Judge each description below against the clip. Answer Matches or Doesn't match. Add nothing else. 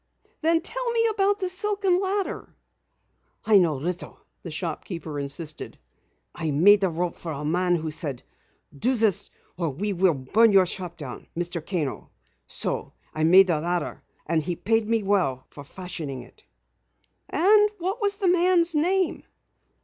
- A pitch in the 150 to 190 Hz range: Matches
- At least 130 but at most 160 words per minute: Matches